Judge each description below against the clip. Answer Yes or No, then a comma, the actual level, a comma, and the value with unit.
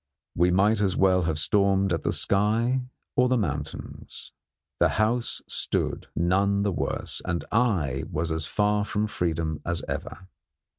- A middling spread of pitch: Yes, average, 3.8 semitones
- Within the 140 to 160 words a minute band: Yes, average, 150 wpm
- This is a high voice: No, very low, 95 Hz